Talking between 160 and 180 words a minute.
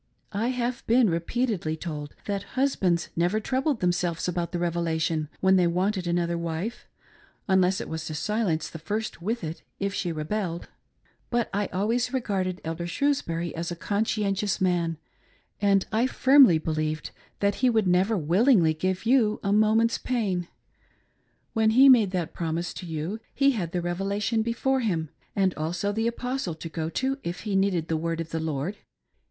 Yes: average, 175 wpm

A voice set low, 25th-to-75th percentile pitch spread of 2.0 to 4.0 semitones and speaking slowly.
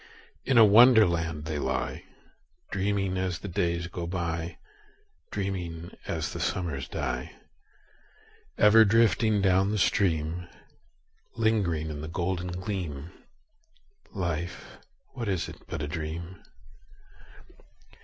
Yes: very low, 90 Hz; average, 3.5 semitones; slow, 110 wpm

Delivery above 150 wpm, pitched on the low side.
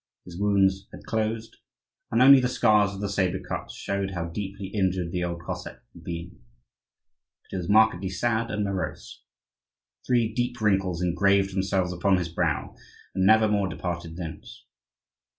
Yes: average, 160 wpm; very low, 95 Hz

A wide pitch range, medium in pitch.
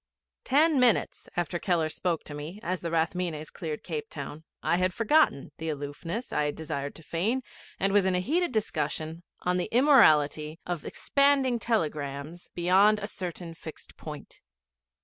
Yes: wide, 5.8 semitones; medium, 175 Hz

